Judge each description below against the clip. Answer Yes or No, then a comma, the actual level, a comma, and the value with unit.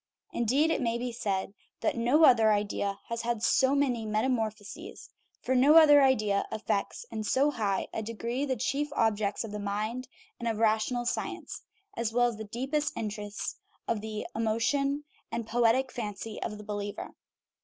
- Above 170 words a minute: No, average, 165 wpm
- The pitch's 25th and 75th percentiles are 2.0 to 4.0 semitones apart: Yes, average, 3.4 semitones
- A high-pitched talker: Yes, high, 230 Hz